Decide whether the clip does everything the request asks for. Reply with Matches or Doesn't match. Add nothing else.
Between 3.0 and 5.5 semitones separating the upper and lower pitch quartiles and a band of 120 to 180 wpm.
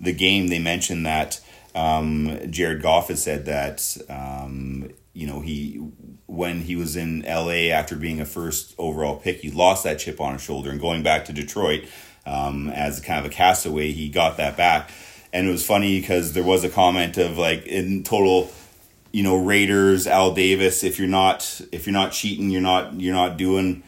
Doesn't match